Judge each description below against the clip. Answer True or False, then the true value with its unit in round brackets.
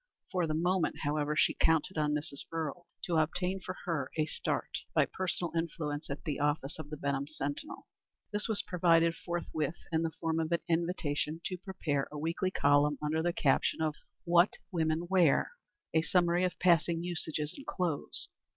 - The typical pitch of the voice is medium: True (165 Hz)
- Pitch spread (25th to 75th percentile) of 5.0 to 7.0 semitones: False (2.6 semitones)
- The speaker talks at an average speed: True (175 wpm)